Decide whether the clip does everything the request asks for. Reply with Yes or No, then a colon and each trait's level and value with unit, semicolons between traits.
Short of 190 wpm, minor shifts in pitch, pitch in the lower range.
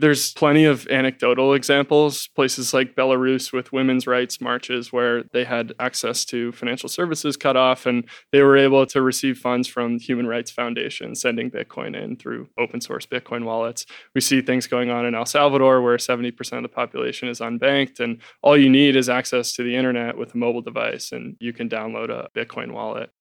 No: average, 195 wpm; narrow, 2.0 semitones; low, 125 Hz